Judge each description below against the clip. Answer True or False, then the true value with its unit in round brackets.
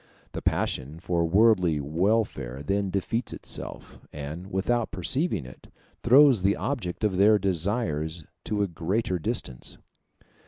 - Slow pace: True (125 wpm)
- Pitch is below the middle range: True (95 Hz)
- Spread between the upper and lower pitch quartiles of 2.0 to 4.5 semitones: False (5.0 semitones)